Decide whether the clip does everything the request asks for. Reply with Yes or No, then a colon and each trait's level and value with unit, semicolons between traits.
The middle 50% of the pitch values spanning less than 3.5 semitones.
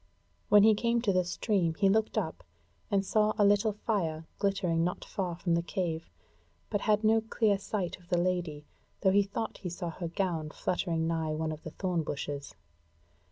No: average, 3.8 semitones